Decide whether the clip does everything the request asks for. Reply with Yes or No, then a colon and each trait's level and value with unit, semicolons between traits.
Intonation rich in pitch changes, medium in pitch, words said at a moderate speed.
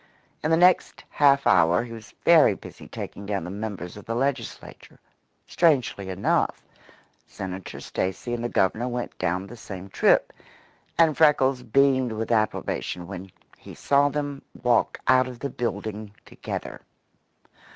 No: wide, 5.8 semitones; low, 120 Hz; average, 145 wpm